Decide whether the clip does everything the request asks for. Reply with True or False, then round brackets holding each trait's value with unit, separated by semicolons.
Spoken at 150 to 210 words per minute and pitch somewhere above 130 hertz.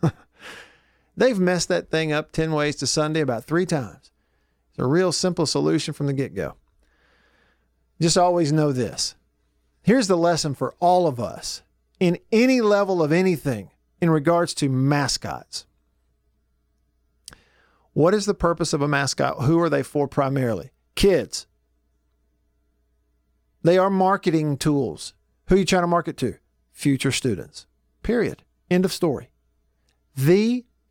False (140 wpm; 140 Hz)